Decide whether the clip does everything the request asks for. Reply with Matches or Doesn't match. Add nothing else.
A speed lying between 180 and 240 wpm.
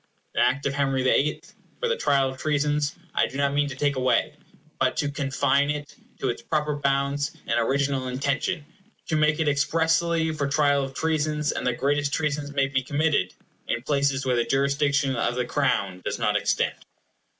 Matches